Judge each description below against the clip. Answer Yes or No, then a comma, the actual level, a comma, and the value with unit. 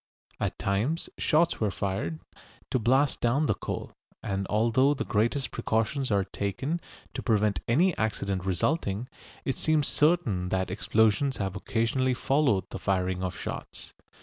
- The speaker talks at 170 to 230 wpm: No, average, 145 wpm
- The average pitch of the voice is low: Yes, low, 110 Hz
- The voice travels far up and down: Yes, wide, 5.8 semitones